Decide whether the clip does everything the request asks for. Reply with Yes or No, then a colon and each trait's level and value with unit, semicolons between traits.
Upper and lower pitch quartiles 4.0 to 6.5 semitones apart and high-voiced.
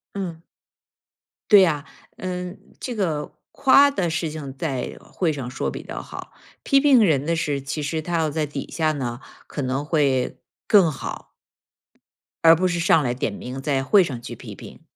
No: average, 4.6 semitones; medium, 155 Hz